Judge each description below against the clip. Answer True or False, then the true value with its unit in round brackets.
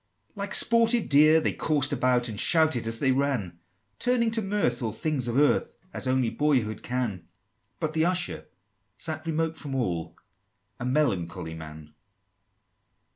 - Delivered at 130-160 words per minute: True (150 wpm)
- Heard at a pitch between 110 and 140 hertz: True (135 Hz)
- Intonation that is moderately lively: False (5.9 semitones)